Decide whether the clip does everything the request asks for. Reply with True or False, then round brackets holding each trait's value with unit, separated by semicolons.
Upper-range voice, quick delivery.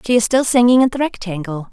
True (225 Hz; 245 wpm)